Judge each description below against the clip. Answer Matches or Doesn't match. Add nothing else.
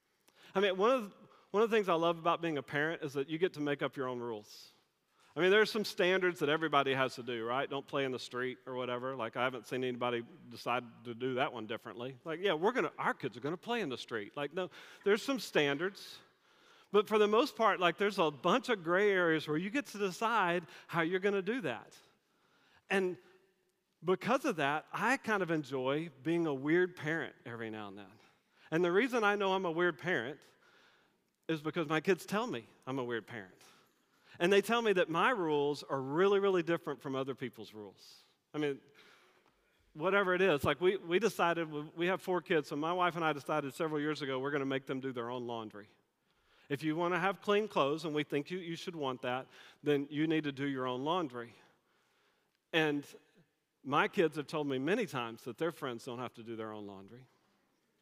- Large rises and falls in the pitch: Matches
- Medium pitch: Matches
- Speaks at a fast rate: Matches